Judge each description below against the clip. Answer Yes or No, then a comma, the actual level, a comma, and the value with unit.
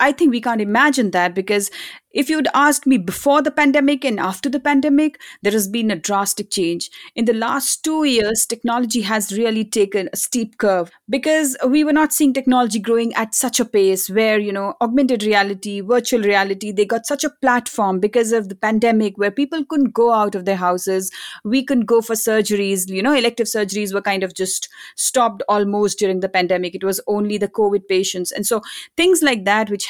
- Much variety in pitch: No, average, 4.3 semitones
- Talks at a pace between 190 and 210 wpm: Yes, fast, 205 wpm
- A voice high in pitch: Yes, high, 220 Hz